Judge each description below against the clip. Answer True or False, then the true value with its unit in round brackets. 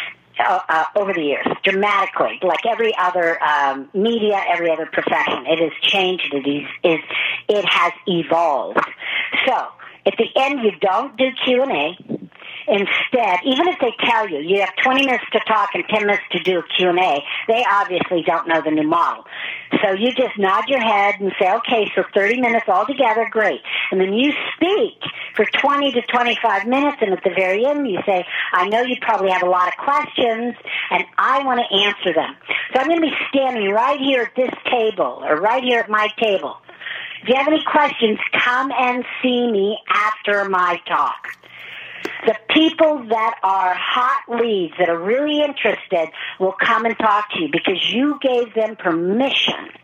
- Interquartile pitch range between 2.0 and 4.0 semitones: False (5.2 semitones)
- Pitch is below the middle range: False (215 Hz)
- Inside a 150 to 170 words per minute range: False (185 wpm)